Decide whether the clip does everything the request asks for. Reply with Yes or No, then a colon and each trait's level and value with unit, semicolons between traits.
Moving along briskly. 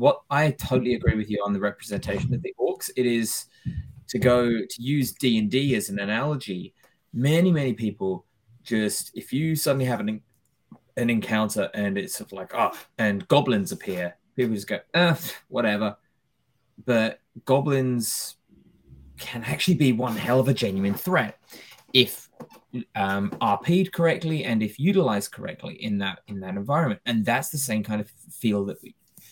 No: average, 170 wpm